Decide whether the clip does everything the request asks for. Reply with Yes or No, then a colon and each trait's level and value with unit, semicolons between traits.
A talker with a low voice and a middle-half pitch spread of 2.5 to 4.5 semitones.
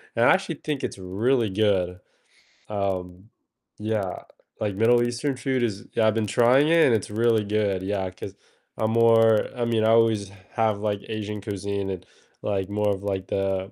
Yes: low, 105 Hz; average, 2.8 semitones